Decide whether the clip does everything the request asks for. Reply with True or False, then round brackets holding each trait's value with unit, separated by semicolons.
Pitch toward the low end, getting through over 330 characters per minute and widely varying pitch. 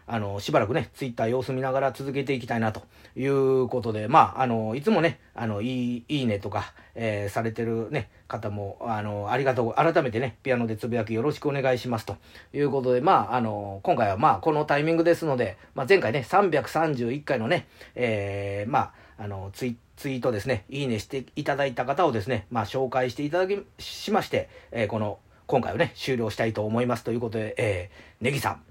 False (125 Hz; 410 characters per minute; 3.9 semitones)